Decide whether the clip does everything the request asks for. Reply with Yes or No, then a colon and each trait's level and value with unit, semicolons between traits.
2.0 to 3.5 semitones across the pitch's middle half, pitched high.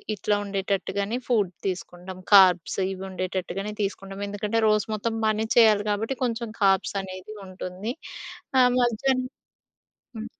Yes: average, 2.8 semitones; high, 205 Hz